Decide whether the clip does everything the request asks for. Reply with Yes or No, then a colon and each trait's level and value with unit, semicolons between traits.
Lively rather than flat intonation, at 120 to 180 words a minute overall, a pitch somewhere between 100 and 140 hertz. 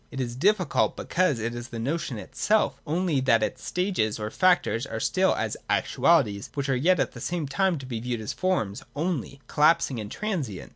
No: wide, 7.2 semitones; average, 195 wpm; low, 135 Hz